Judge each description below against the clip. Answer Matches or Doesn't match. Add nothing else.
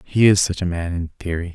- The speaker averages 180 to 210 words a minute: Doesn't match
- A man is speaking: Matches